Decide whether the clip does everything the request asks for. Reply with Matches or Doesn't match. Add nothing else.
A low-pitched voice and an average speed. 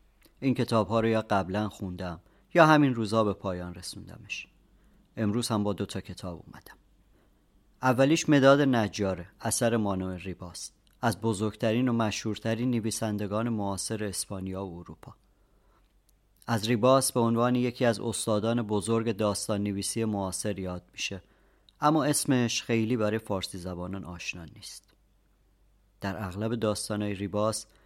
Matches